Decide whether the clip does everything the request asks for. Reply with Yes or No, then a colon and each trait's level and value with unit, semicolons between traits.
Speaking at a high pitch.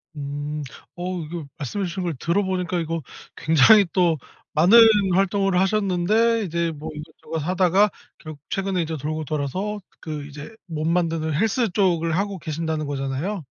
No: medium, 170 Hz